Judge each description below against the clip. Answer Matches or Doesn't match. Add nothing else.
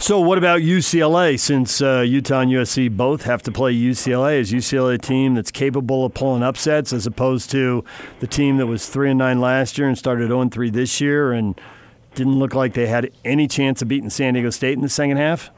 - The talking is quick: Matches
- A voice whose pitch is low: Matches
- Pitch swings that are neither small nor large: Doesn't match